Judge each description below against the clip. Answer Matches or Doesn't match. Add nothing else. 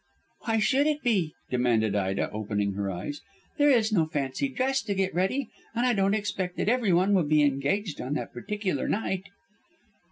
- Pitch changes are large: Matches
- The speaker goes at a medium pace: Matches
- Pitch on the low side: Doesn't match